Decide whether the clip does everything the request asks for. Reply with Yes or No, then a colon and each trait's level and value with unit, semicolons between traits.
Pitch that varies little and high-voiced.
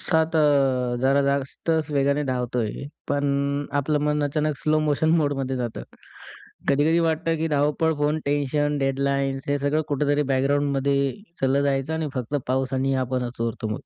No: narrow, 1.7 semitones; medium, 140 Hz